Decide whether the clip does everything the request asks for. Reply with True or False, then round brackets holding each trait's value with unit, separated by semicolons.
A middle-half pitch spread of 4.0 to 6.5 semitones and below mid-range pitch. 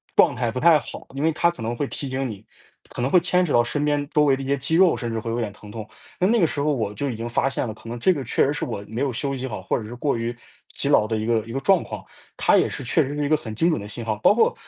True (4.3 semitones; 130 Hz)